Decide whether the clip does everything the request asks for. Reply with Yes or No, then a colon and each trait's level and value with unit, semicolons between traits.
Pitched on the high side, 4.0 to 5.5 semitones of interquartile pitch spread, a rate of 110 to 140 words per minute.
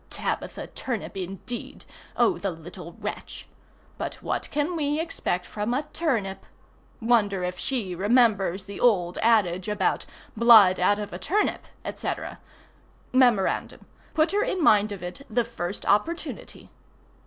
Yes: high, 210 Hz; average, 5.2 semitones; slow, 135 wpm